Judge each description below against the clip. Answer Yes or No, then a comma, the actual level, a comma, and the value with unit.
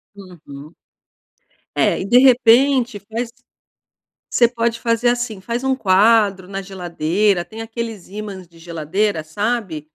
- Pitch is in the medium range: No, high, 210 Hz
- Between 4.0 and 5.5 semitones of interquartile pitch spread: Yes, average, 4.3 semitones